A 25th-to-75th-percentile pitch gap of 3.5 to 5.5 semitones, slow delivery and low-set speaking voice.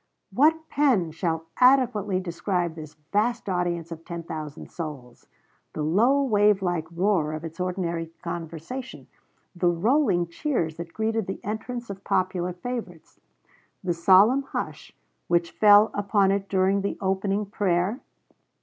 No: average, 4.0 semitones; slow, 130 wpm; high, 190 Hz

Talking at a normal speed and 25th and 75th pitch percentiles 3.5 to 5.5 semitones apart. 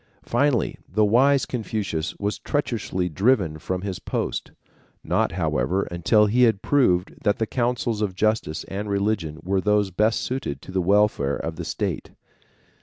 Yes: average, 155 wpm; average, 3.9 semitones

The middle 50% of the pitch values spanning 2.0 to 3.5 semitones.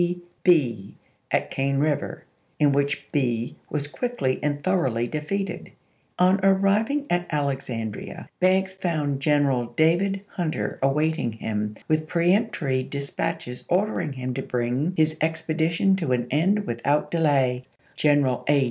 No: average, 4.9 semitones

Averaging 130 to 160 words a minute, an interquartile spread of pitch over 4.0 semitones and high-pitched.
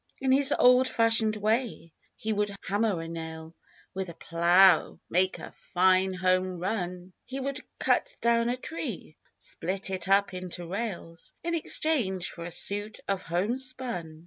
Yes: average, 155 wpm; average, 4.8 semitones; high, 195 Hz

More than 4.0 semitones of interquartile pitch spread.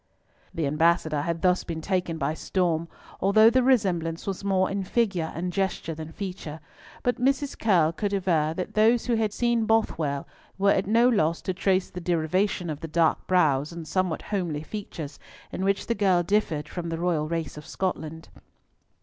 No: average, 3.7 semitones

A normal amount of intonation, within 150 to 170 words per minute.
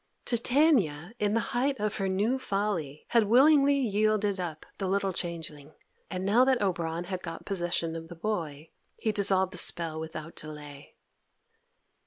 Yes: average, 4.8 semitones; average, 155 wpm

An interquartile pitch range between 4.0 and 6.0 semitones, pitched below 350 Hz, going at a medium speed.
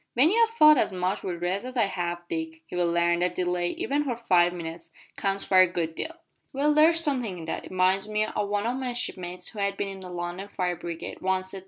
No: average, 5.0 semitones; medium, 185 Hz; fast, 245 wpm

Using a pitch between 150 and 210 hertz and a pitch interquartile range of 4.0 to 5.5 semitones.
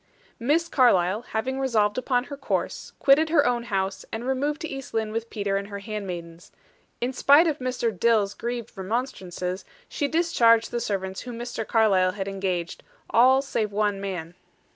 No: high, 225 Hz; average, 4.7 semitones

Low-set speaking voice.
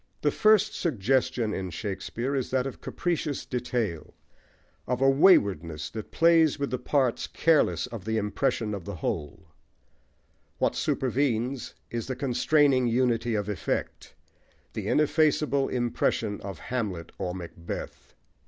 Yes: low, 120 Hz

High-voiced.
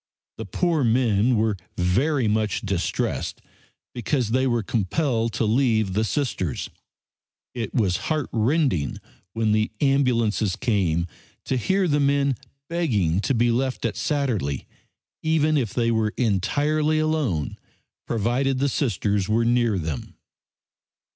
No: low, 115 Hz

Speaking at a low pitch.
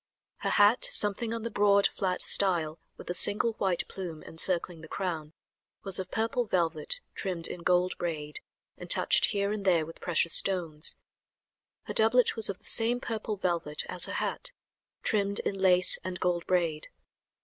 No: medium, 185 Hz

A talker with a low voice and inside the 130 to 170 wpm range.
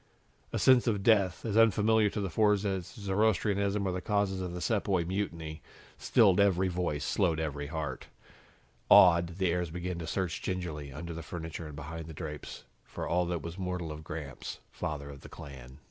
No: very low, 90 Hz; average, 185 wpm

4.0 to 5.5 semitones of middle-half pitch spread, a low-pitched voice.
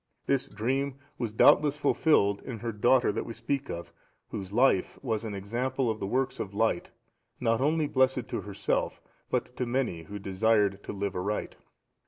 Yes: average, 4.5 semitones; low, 115 Hz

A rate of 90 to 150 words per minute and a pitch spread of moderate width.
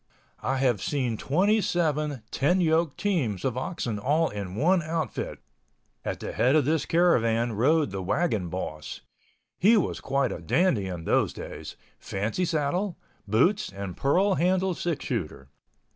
No: average, 145 wpm; wide, 8.1 semitones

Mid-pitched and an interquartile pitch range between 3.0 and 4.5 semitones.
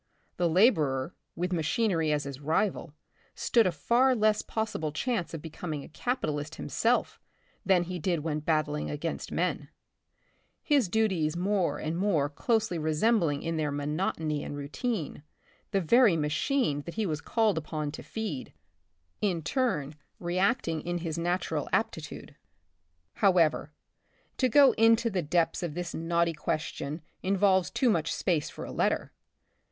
No: medium, 170 Hz; wide, 5.4 semitones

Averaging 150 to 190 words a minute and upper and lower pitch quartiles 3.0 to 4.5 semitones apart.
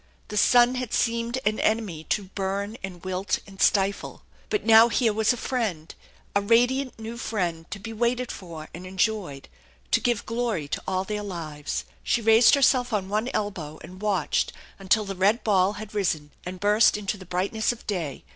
Yes: average, 185 wpm; average, 3.6 semitones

